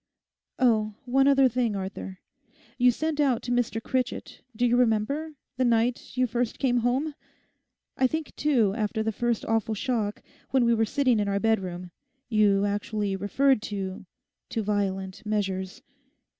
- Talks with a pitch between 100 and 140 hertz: No, high, 225 Hz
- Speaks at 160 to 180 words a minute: No, average, 145 wpm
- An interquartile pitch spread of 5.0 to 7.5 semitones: No, average, 3.6 semitones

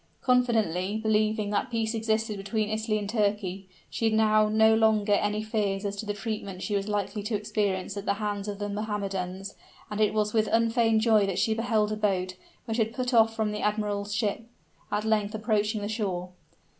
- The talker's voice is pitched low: No, high, 210 Hz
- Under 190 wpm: No, average, 195 wpm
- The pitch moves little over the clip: Yes, narrow, 1.5 semitones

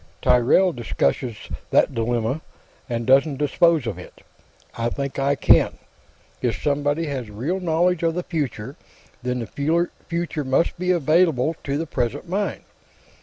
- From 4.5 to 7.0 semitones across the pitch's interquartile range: Yes, average, 5.3 semitones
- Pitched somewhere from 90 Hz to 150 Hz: Yes, medium, 140 Hz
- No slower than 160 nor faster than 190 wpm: No, average, 140 wpm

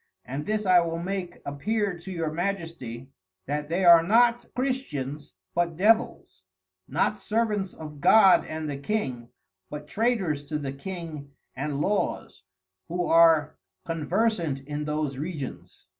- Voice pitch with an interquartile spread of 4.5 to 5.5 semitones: Yes, average, 4.9 semitones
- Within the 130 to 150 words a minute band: Yes, slow, 135 wpm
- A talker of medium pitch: Yes, medium, 165 Hz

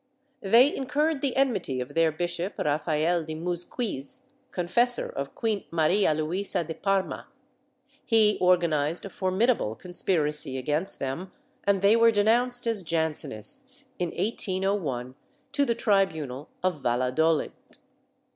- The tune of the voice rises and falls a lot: Yes, wide, 5.9 semitones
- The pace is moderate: No, slow, 120 wpm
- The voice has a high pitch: No, medium, 180 Hz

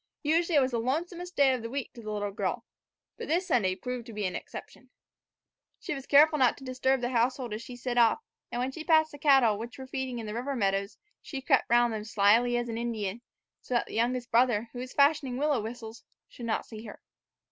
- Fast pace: Yes, fast, 235 wpm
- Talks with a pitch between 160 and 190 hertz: No, high, 245 Hz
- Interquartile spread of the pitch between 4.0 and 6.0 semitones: No, average, 3.1 semitones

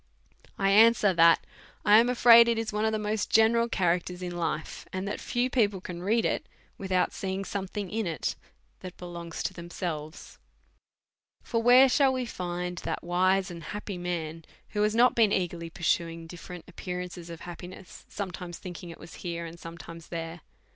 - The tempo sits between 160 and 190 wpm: Yes, average, 180 wpm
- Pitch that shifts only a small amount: No, average, 3.7 semitones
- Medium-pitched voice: Yes, medium, 180 Hz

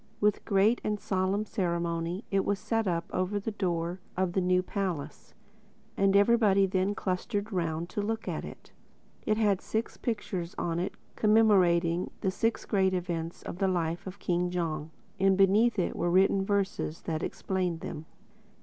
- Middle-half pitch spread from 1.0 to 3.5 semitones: Yes, average, 2.8 semitones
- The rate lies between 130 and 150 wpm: No, average, 165 wpm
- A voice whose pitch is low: No, high, 190 Hz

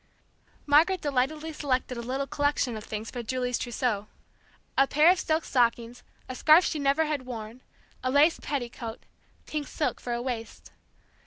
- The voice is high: Yes, very high, 260 Hz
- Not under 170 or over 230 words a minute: No, average, 160 wpm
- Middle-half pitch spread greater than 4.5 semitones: No, average, 3.9 semitones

